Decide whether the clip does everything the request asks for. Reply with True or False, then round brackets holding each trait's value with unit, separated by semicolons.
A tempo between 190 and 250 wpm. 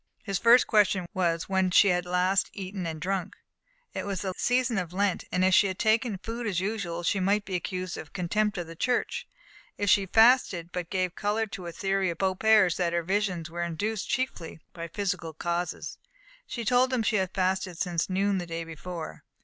True (200 wpm)